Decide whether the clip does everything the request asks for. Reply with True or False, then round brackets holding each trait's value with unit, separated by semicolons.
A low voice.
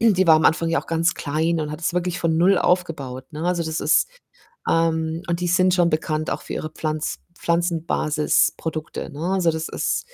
False (165 Hz)